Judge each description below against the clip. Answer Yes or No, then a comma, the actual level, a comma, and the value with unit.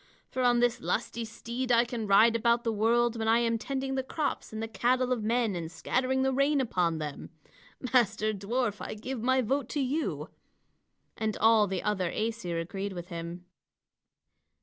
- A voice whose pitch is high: Yes, high, 230 Hz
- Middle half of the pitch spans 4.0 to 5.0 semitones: No, average, 3.5 semitones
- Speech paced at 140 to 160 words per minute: No, average, 180 wpm